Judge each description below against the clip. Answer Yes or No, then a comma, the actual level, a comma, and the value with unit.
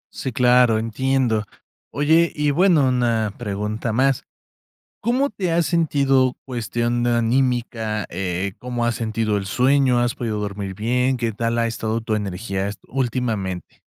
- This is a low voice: Yes, low, 120 Hz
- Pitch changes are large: No, average, 3.5 semitones